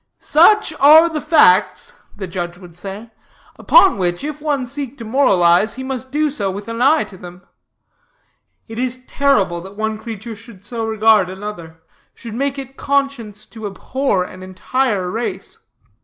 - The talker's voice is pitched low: No, high, 225 Hz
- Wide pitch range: Yes, wide, 6.1 semitones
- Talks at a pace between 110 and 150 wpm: No, average, 160 wpm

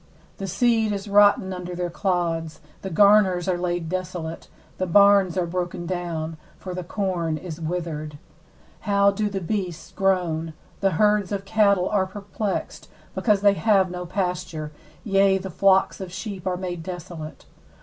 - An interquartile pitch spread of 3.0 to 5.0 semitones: No, narrow, 2.4 semitones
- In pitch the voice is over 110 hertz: Yes, medium, 185 Hz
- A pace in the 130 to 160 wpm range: Yes, average, 155 wpm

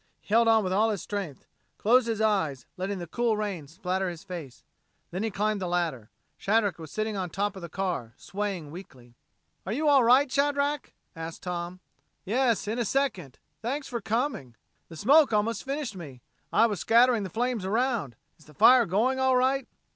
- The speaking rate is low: No, average, 195 wpm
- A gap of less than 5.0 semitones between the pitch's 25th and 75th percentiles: No, wide, 5.4 semitones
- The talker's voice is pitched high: Yes, high, 205 Hz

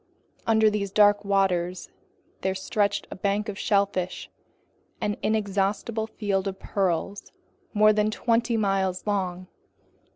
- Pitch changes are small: Yes, narrow, 1.7 semitones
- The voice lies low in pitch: No, high, 200 Hz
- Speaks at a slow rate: Yes, slow, 120 wpm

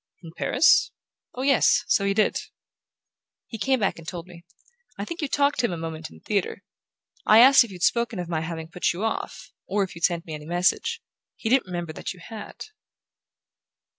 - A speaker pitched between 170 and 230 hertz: Yes, medium, 185 Hz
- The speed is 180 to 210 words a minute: Yes, average, 200 wpm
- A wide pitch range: Yes, wide, 5.7 semitones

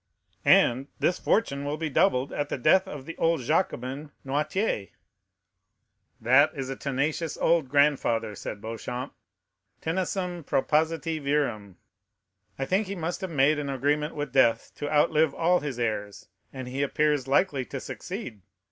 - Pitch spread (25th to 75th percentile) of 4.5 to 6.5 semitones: No, average, 3.7 semitones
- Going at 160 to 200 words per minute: No, average, 150 wpm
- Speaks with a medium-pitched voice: Yes, medium, 145 Hz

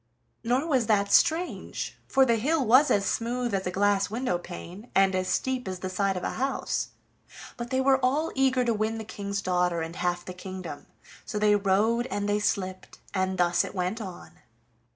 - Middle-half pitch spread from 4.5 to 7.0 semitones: Yes, average, 5.0 semitones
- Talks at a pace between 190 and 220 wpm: Yes, average, 195 wpm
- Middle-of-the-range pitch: No, high, 205 Hz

